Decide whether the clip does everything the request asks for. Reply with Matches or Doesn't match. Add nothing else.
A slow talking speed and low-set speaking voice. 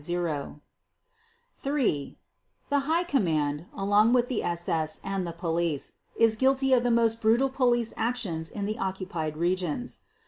Doesn't match